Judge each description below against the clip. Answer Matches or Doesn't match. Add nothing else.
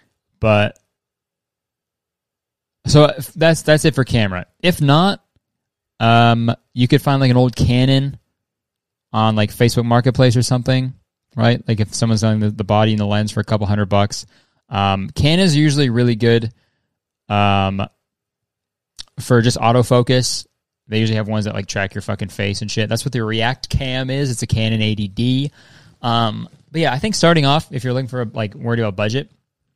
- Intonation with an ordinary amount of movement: Matches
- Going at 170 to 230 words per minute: Matches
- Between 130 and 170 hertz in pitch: Doesn't match